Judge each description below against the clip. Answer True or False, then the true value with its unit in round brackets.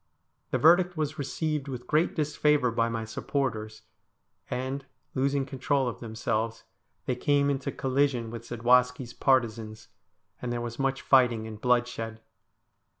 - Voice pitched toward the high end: False (125 Hz)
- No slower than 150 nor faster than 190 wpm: False (135 wpm)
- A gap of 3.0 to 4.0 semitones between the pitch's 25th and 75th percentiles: True (3.3 semitones)